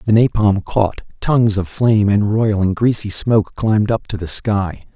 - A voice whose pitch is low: Yes, low, 105 Hz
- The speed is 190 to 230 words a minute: No, average, 180 wpm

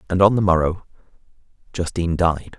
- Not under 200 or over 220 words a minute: No, average, 140 wpm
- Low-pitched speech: Yes, very low, 90 Hz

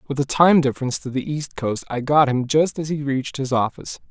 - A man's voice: Yes, male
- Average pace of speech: No, fast, 250 wpm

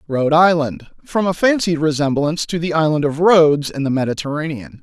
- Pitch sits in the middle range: Yes, medium, 155 Hz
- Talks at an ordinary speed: Yes, average, 160 wpm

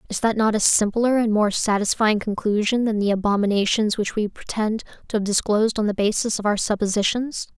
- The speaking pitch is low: No, high, 215 Hz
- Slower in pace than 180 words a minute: No, average, 190 wpm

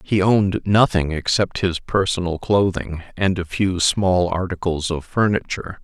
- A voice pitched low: Yes, very low, 90 Hz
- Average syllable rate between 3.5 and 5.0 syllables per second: Yes, 4.5 syllables/s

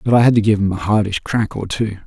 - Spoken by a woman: No, male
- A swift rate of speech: Yes, fast, 320 wpm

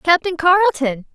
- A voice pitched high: Yes, very high, 315 Hz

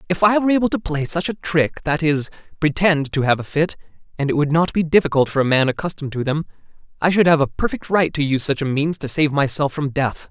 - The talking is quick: Yes, fast, 245 wpm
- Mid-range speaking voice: Yes, medium, 155 Hz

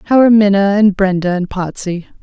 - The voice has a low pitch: No, high, 195 Hz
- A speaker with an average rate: Yes, average, 190 wpm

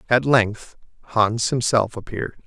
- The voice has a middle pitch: No, low, 110 Hz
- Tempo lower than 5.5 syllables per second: Yes, 4.4 syllables/s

